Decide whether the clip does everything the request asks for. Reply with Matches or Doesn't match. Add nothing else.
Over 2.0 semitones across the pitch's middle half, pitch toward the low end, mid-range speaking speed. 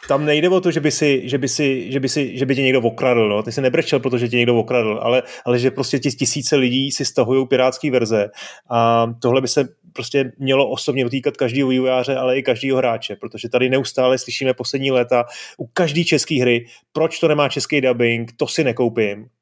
Doesn't match